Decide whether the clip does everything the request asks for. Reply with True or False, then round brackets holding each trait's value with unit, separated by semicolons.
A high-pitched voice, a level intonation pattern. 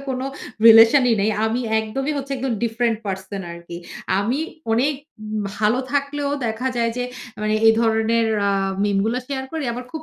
False (230 Hz; 3.3 semitones)